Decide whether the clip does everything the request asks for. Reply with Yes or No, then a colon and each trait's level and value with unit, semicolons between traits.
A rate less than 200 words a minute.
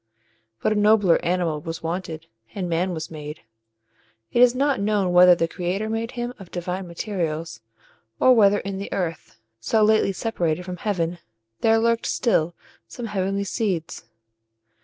Yes: average, 155 wpm